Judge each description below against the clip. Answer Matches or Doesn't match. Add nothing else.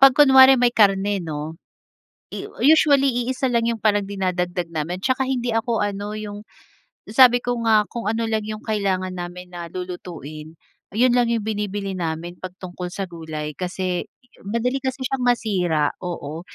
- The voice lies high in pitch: Matches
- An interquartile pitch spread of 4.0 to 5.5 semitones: Matches